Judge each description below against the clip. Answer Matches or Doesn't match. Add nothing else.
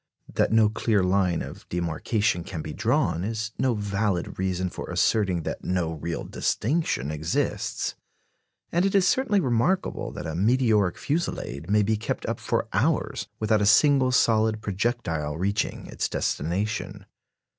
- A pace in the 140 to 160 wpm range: Matches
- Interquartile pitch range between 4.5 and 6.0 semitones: Matches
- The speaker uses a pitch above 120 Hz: Doesn't match